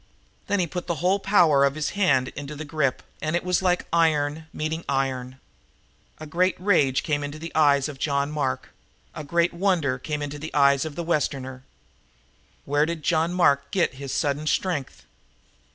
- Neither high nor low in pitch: Yes, medium, 150 Hz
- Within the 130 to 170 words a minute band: No, average, 185 wpm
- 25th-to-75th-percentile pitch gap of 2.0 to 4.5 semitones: Yes, average, 3.4 semitones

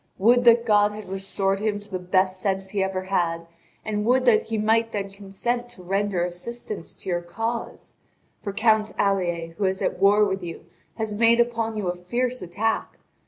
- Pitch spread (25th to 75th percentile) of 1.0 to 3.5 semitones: Yes, average, 3.0 semitones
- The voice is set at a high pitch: Yes, high, 205 Hz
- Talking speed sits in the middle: Yes, average, 190 wpm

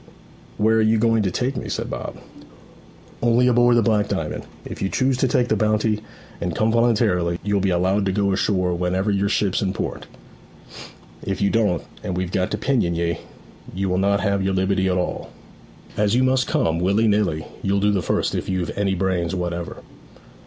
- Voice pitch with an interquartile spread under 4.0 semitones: Yes, average, 3.1 semitones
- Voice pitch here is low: Yes, low, 100 Hz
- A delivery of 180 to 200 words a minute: Yes, average, 195 wpm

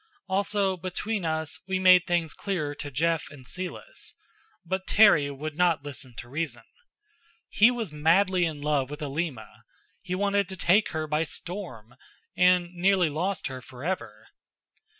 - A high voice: No, medium, 170 Hz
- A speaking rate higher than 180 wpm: No, average, 150 wpm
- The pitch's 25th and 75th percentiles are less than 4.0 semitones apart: No, average, 4.4 semitones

